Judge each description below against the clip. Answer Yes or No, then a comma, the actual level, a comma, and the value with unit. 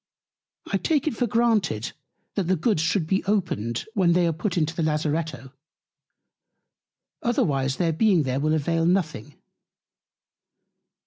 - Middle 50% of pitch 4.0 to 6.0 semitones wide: Yes, average, 4.5 semitones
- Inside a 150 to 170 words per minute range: No, slow, 135 wpm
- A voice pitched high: No, medium, 165 Hz